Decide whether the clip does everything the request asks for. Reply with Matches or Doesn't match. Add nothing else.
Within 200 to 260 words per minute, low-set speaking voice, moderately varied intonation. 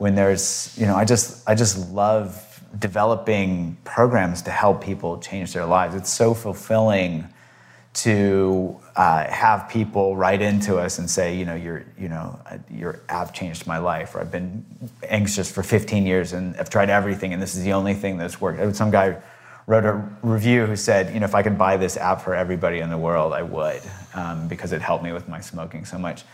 Matches